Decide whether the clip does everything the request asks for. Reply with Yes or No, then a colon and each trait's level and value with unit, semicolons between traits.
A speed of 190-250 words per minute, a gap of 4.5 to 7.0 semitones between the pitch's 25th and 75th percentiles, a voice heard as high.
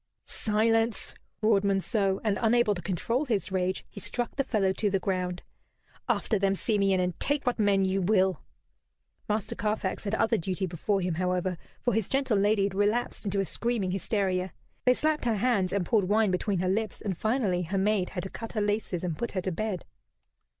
No: average, 195 wpm; average, 2.9 semitones; high, 200 Hz